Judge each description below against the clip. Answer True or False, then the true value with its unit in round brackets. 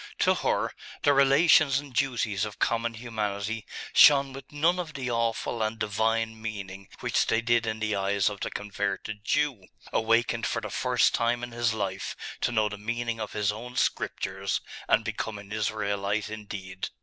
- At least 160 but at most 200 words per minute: True (175 wpm)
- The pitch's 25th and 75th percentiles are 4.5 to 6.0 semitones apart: False (2.7 semitones)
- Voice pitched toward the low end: True (110 Hz)